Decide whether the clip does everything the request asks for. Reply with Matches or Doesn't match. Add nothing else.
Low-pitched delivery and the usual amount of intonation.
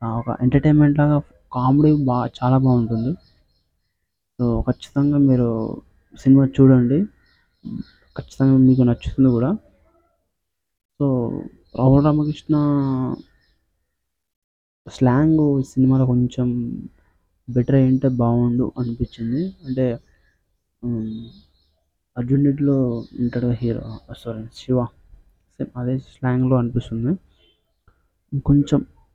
Matches